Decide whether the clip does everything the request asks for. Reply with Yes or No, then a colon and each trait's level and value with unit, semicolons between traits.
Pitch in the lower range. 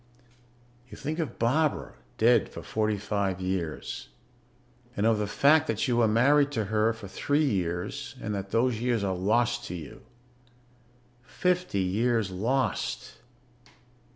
Yes: low, 110 Hz